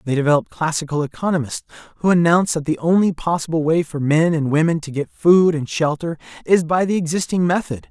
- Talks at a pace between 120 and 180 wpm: No, average, 190 wpm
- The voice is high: No, medium, 160 Hz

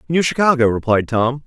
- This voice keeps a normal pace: Yes, average, 165 wpm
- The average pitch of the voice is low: Yes, low, 130 Hz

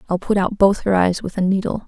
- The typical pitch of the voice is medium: No, high, 195 Hz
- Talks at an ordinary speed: No, fast, 285 wpm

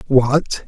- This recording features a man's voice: Yes, male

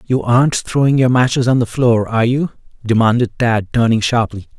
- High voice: No, low, 120 Hz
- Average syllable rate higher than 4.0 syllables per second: Yes, 5.4 syllables/s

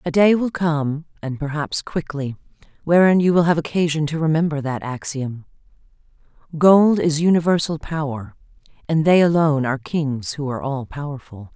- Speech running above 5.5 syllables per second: No, 5.1 syllables/s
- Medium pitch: Yes, medium, 150 Hz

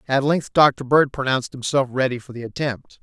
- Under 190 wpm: No, average, 200 wpm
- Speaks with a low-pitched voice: Yes, low, 130 Hz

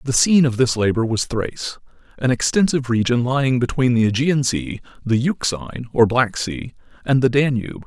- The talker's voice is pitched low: Yes, low, 125 Hz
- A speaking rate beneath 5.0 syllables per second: No, 5.6 syllables/s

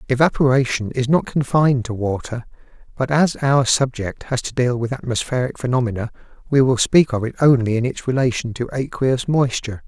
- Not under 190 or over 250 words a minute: No, average, 170 wpm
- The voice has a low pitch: Yes, low, 125 Hz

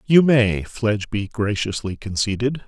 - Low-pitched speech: Yes, low, 110 Hz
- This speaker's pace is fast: No, slow, 110 wpm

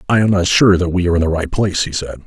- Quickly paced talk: Yes, fast, 345 wpm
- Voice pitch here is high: No, very low, 90 Hz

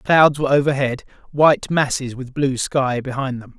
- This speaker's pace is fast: No, average, 165 wpm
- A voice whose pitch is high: No, low, 135 Hz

